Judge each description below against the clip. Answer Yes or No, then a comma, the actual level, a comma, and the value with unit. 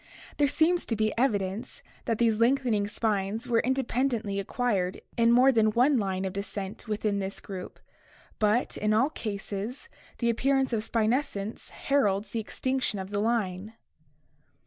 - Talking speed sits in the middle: Yes, average, 150 wpm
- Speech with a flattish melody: No, average, 3.5 semitones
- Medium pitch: No, high, 220 Hz